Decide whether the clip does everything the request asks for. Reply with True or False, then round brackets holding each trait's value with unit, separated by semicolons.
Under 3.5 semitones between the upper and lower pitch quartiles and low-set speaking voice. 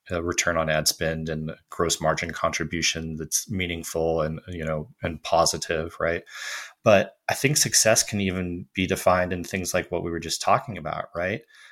True (2.4 semitones; 85 Hz)